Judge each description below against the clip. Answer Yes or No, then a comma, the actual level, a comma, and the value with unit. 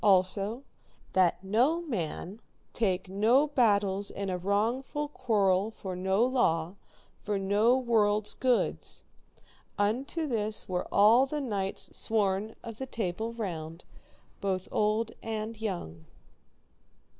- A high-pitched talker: Yes, high, 210 Hz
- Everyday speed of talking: No, slow, 120 wpm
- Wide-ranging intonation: No, average, 3.5 semitones